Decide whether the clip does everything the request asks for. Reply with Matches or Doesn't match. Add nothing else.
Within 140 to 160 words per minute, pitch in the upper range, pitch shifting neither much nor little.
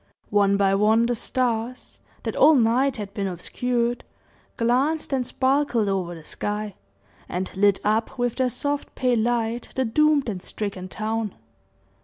Matches